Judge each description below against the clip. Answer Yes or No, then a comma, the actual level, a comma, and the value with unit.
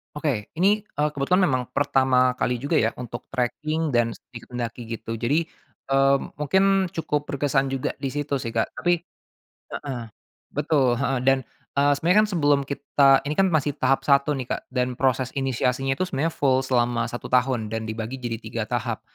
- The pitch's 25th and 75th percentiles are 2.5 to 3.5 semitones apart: Yes, average, 3.2 semitones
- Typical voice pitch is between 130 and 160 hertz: Yes, low, 135 Hz